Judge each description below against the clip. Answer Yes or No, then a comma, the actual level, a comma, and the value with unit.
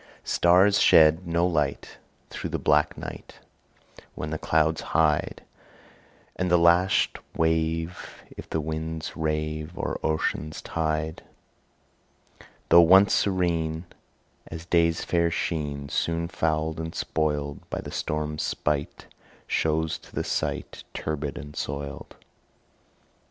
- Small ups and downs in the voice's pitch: Yes, narrow, 1.5 semitones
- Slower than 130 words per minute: Yes, slow, 115 wpm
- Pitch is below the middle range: Yes, very low, 80 Hz